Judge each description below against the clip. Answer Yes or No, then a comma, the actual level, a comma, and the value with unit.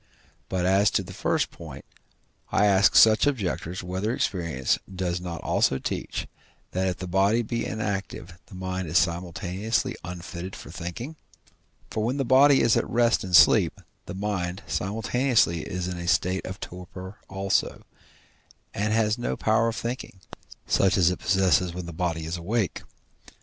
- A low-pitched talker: Yes, very low, 95 Hz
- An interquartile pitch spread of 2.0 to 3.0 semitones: No, average, 3.6 semitones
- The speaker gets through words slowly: No, average, 160 wpm